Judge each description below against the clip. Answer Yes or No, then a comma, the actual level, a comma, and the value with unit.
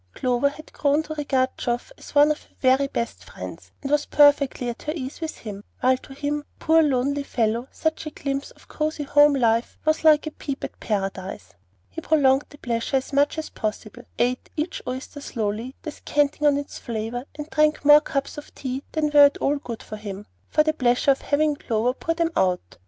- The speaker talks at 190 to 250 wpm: Yes, fast, 205 wpm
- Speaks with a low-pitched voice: No, very high, 280 Hz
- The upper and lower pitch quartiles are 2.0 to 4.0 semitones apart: Yes, average, 3.5 semitones